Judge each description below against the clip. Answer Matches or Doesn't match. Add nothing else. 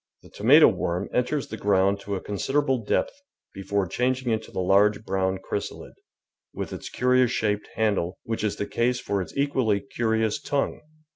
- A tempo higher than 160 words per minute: Matches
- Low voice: Matches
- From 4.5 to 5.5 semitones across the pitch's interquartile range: Doesn't match